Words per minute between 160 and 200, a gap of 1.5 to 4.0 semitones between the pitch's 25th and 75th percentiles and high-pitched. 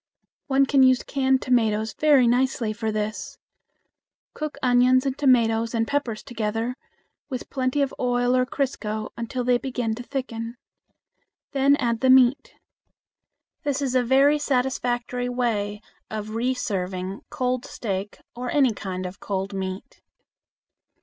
No: slow, 135 wpm; average, 3.1 semitones; high, 245 Hz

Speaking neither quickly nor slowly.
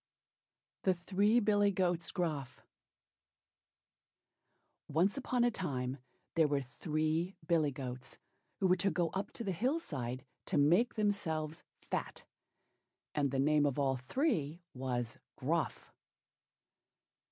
No: slow, 120 wpm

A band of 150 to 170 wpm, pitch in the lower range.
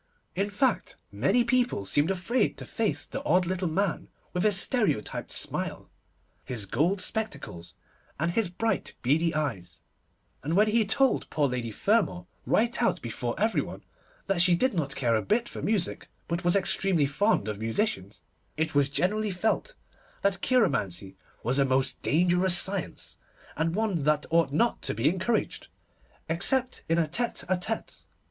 No: average, 160 wpm; medium, 180 Hz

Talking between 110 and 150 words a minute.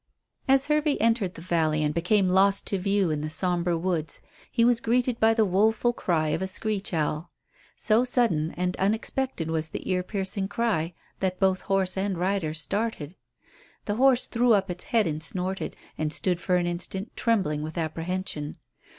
No: average, 175 wpm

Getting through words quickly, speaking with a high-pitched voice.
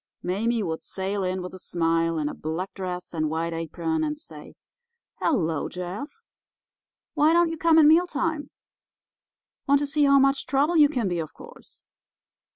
No: average, 165 wpm; high, 225 Hz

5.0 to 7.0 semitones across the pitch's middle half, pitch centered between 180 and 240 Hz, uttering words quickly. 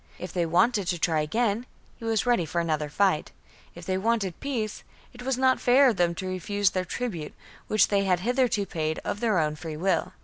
Yes: average, 5.3 semitones; high, 190 Hz; fast, 210 wpm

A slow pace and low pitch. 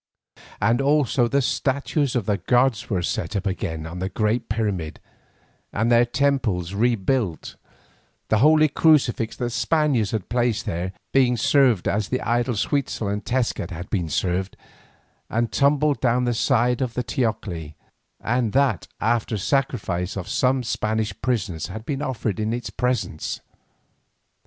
No: average, 145 wpm; low, 115 Hz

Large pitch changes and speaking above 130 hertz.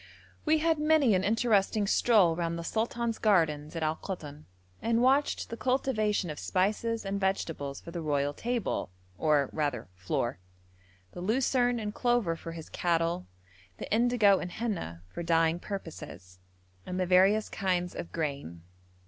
Yes: wide, 6.0 semitones; medium, 185 Hz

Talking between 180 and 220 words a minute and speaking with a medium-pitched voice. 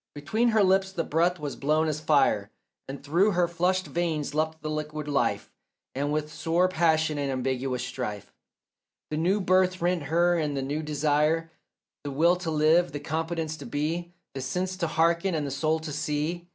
Yes: average, 185 wpm; medium, 155 Hz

